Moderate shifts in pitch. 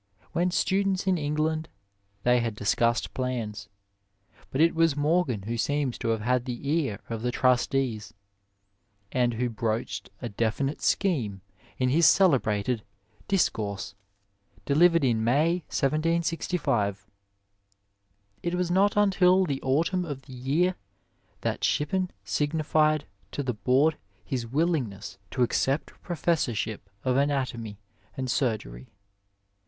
No: wide, 5.9 semitones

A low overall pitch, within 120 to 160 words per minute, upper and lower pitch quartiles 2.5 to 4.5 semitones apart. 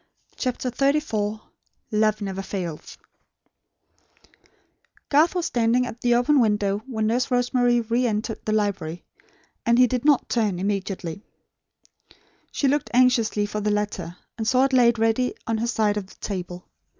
No: high, 225 Hz; average, 150 wpm; average, 3.3 semitones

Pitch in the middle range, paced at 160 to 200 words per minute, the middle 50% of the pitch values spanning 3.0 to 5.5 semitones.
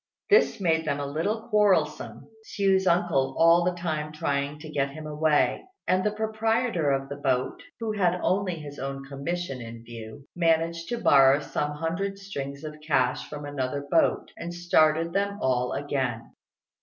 Yes: medium, 155 Hz; average, 165 wpm; average, 4.5 semitones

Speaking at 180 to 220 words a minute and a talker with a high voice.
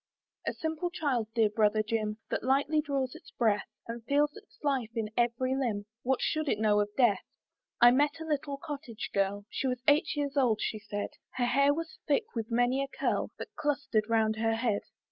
Yes: average, 200 wpm; high, 245 Hz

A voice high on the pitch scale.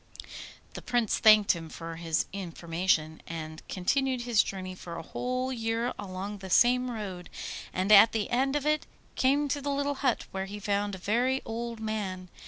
Yes: high, 210 Hz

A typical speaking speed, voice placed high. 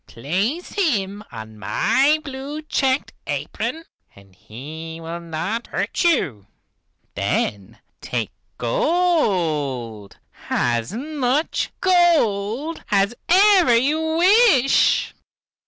No: slow, 90 wpm; high, 225 Hz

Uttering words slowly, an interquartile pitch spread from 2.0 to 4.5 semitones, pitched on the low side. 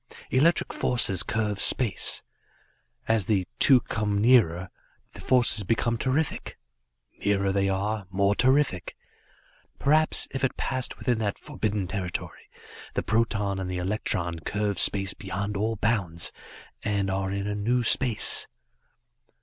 Yes: slow, 130 wpm; average, 3.3 semitones; low, 105 Hz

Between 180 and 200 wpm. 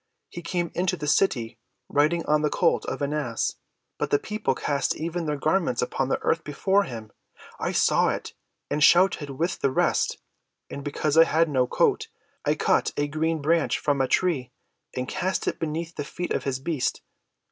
Yes: average, 190 wpm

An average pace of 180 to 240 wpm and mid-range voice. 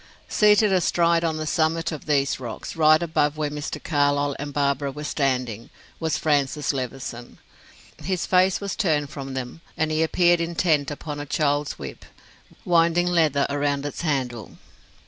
No: average, 155 wpm; medium, 150 Hz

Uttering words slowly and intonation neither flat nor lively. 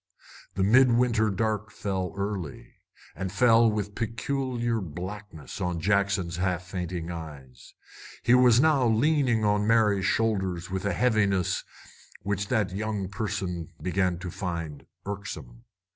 Yes: slow, 125 wpm; average, 3.7 semitones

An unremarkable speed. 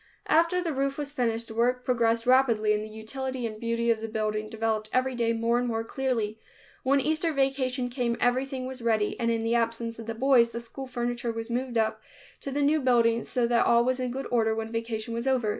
No: fast, 225 wpm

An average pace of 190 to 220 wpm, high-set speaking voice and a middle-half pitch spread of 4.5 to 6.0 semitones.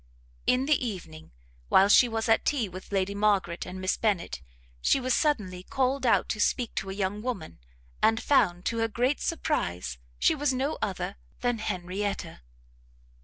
No: average, 170 wpm; high, 210 Hz; average, 5.2 semitones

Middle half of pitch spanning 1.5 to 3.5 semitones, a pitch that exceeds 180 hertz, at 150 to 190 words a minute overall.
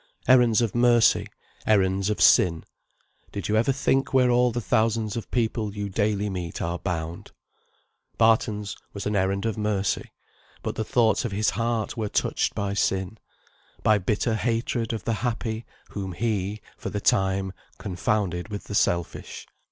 No: average, 2.7 semitones; low, 105 Hz; average, 160 wpm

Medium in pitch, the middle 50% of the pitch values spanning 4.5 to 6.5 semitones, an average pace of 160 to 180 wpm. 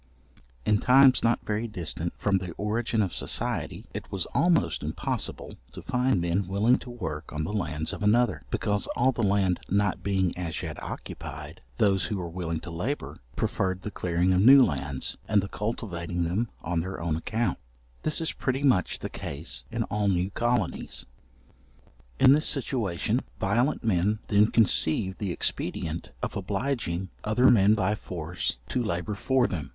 No: low, 100 Hz; average, 5.0 semitones; average, 165 wpm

